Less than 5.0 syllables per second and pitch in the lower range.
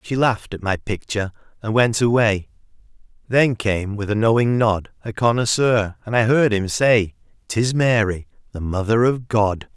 Yes: 4.6 syllables/s; low, 110 Hz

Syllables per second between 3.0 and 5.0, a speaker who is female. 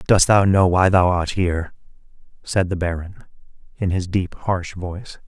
No: 4.6 syllables/s; male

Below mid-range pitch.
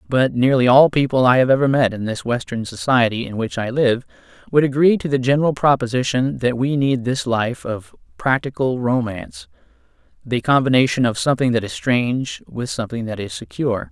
Yes: low, 125 Hz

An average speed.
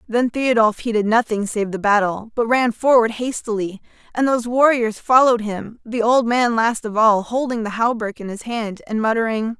Yes: average, 190 wpm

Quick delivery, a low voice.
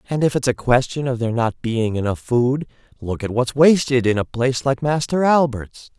Yes: fast, 210 wpm; low, 125 Hz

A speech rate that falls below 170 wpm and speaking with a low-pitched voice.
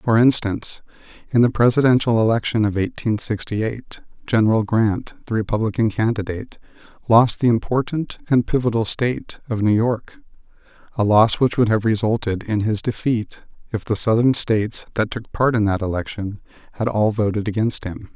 Yes: average, 160 wpm; low, 110 Hz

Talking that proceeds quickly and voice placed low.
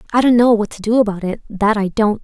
No: fast, 295 wpm; high, 215 Hz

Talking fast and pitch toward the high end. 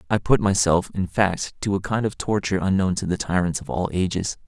No: fast, 230 wpm; very low, 95 Hz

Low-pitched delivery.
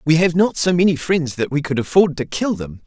No: medium, 160 Hz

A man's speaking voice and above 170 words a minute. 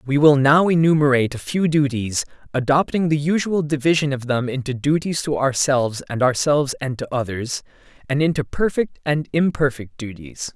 No: male; average, 160 wpm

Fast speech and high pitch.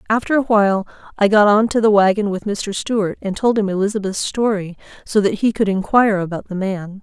Yes: fast, 215 wpm; high, 205 Hz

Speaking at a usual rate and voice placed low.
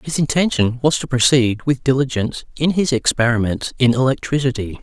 Yes: average, 150 wpm; low, 130 Hz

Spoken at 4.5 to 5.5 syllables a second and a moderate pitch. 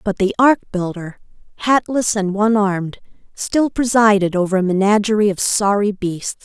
No: 5.0 syllables/s; high, 205 Hz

